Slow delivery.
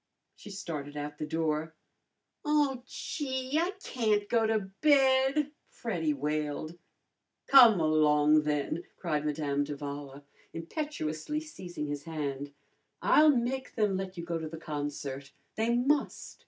Yes: slow, 125 wpm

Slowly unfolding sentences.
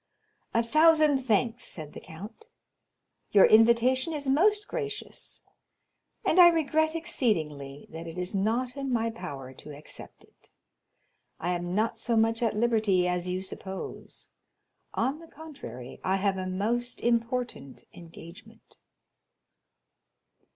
Yes: slow, 130 wpm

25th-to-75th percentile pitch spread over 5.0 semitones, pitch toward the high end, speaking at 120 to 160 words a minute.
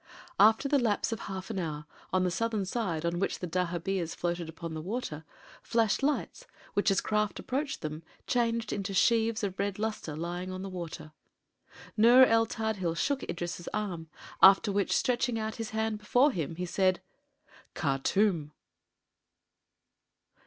No: average, 4.4 semitones; high, 195 Hz; average, 150 wpm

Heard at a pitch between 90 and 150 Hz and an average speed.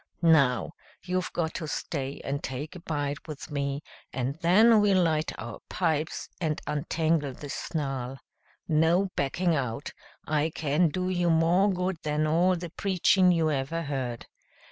No: medium, 160 Hz; average, 150 wpm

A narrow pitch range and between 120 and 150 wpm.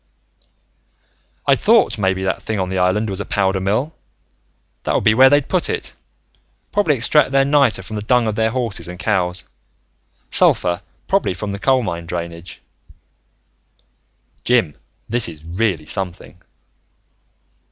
No: average, 5.3 semitones; average, 140 wpm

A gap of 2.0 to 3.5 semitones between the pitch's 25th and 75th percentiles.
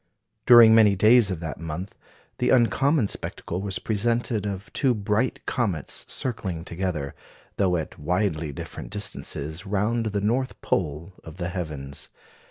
No: average, 5.3 semitones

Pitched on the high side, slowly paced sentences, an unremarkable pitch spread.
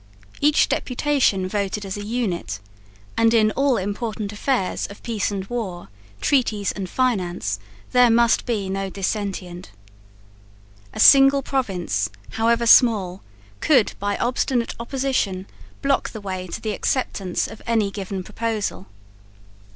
Yes: high, 210 Hz; slow, 130 wpm; average, 4.1 semitones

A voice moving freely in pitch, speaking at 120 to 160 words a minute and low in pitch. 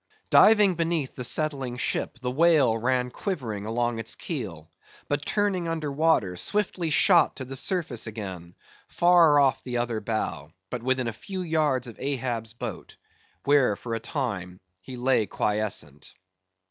Yes: wide, 5.9 semitones; average, 150 wpm; low, 130 Hz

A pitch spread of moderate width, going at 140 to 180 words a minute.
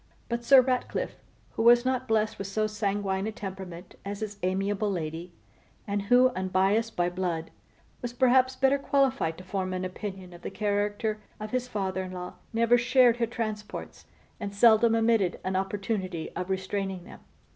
Yes: average, 3.7 semitones; average, 165 wpm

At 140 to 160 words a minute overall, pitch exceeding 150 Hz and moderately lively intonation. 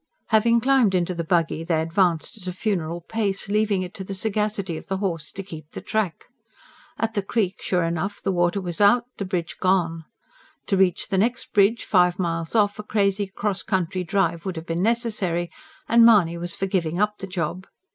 No: average, 200 wpm; high, 190 Hz; average, 3.4 semitones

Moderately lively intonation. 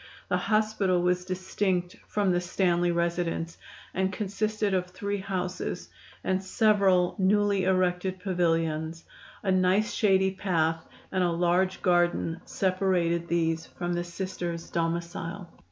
No: narrow, 1.9 semitones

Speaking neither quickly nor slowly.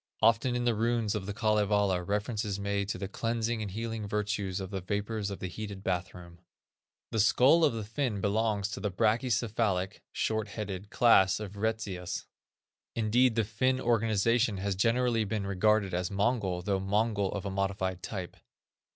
Yes: average, 170 wpm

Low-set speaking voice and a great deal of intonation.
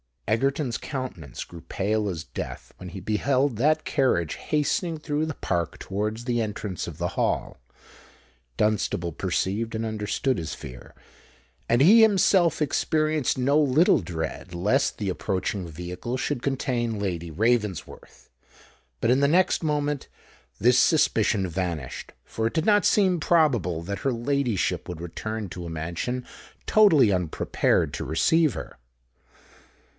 Yes: low, 115 Hz; wide, 7.8 semitones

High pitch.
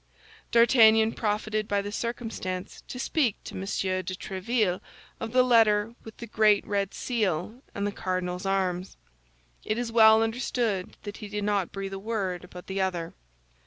Yes: high, 210 Hz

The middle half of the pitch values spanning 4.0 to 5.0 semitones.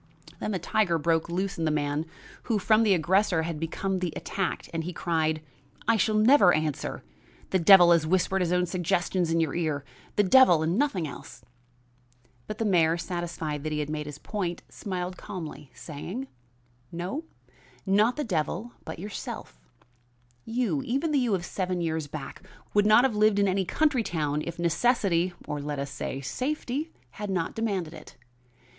Yes: average, 4.7 semitones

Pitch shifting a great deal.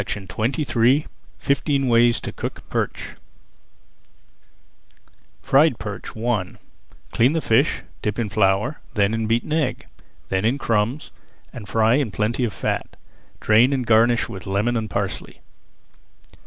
No: average, 3.3 semitones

